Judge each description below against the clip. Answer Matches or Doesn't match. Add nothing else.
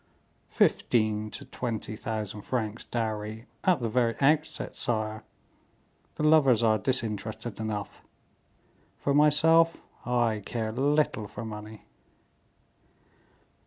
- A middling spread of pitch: Matches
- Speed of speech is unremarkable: Doesn't match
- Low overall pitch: Matches